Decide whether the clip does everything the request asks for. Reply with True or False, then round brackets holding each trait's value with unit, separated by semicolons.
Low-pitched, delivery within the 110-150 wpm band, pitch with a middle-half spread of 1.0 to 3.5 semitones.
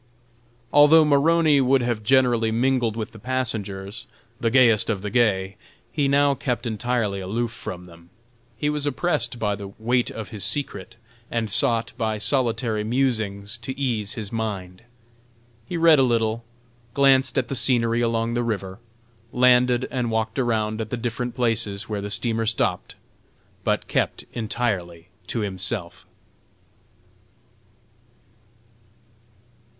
True (115 Hz; 135 wpm; 3.0 semitones)